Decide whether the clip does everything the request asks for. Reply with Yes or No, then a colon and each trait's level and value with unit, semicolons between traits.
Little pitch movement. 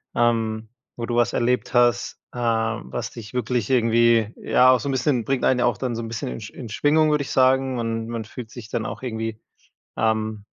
Yes: narrow, 2.0 semitones